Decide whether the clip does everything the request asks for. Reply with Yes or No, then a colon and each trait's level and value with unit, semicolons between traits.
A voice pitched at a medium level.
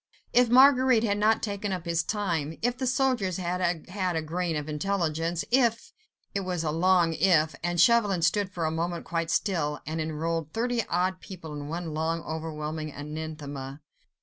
Yes: medium, 170 Hz